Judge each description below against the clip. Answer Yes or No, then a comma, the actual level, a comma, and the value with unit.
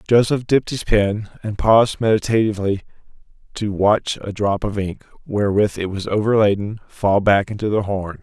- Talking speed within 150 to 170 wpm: Yes, average, 160 wpm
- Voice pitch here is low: Yes, low, 105 Hz